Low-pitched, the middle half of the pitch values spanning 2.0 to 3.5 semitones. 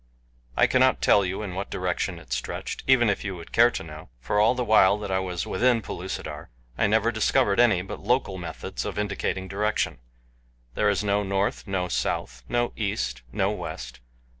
Yes: low, 100 Hz; average, 3.0 semitones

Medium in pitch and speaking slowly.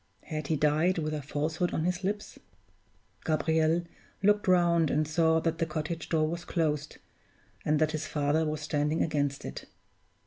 No: medium, 155 Hz; average, 165 wpm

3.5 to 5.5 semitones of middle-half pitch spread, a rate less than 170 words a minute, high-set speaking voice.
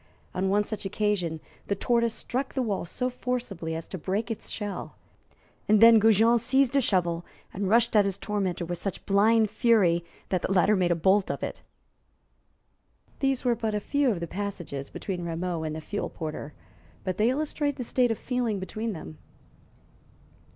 No: average, 4.5 semitones; average, 180 wpm; high, 205 Hz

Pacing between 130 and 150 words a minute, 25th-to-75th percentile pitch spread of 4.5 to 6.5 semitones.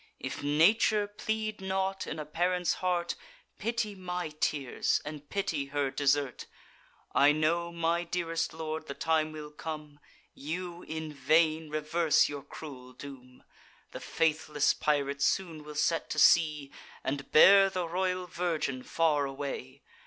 No: average, 140 wpm; average, 3.4 semitones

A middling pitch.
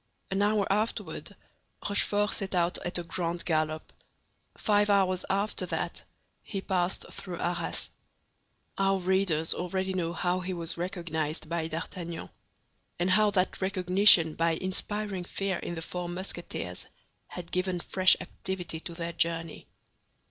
Yes: medium, 180 Hz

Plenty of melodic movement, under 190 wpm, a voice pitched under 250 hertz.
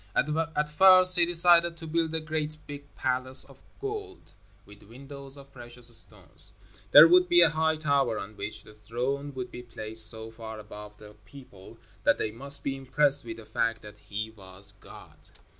Yes: wide, 6.0 semitones; average, 180 wpm; low, 135 Hz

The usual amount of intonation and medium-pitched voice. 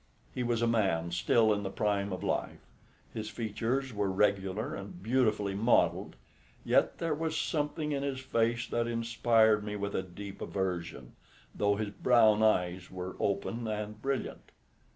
No: average, 3.0 semitones; low, 110 Hz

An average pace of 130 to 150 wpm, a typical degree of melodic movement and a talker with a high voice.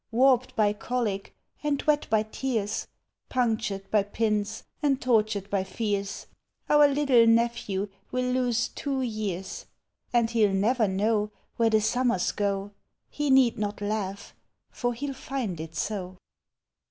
Yes: average, 140 wpm; average, 3.7 semitones; high, 220 Hz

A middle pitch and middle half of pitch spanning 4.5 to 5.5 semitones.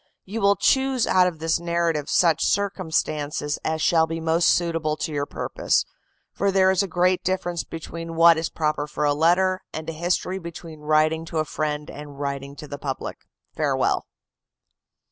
No: medium, 165 Hz; average, 2.8 semitones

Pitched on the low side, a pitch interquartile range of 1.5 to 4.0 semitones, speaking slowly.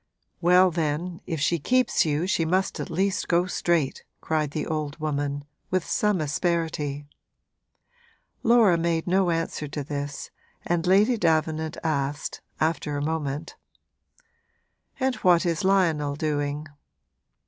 No: medium, 160 Hz; average, 3.3 semitones; slow, 125 wpm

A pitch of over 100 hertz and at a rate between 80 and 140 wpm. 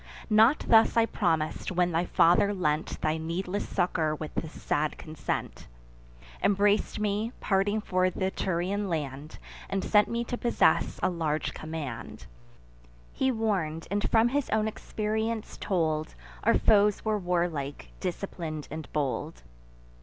Yes: medium, 185 Hz; slow, 135 wpm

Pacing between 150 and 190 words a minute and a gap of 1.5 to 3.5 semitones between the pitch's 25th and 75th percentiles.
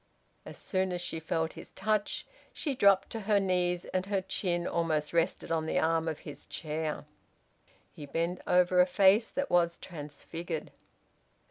Yes: average, 160 wpm; average, 2.7 semitones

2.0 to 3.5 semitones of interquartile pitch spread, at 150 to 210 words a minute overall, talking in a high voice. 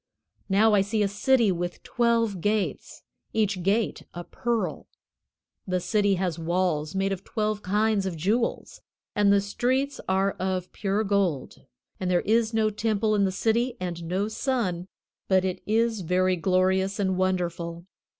Yes: average, 3.0 semitones; average, 155 wpm; high, 195 Hz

